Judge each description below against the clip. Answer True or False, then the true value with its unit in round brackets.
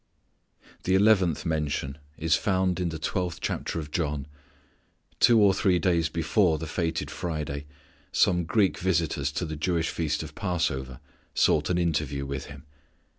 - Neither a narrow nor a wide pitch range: True (3.3 semitones)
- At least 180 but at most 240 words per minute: False (150 wpm)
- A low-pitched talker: True (80 Hz)